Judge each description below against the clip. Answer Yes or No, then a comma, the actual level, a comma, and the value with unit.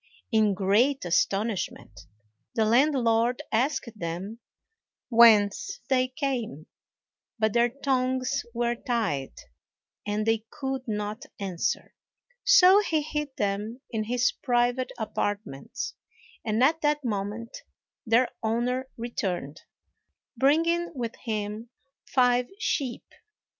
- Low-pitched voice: No, high, 235 Hz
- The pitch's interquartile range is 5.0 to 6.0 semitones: No, average, 3.7 semitones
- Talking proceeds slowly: Yes, slow, 100 wpm